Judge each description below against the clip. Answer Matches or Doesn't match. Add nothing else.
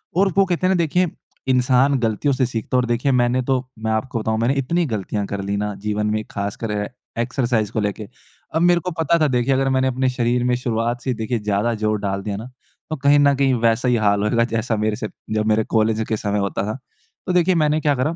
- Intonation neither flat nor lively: Matches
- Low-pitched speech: Matches